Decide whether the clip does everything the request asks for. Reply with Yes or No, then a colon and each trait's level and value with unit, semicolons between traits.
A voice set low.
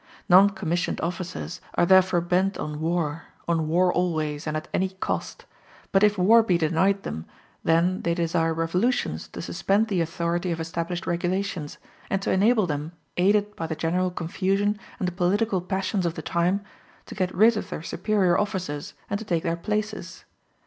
No: medium, 180 Hz